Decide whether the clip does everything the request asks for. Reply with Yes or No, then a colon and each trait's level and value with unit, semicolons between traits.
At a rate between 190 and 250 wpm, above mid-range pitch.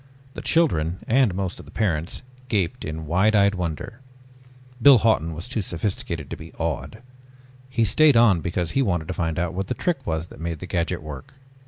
No: average, 195 wpm; very low, 90 Hz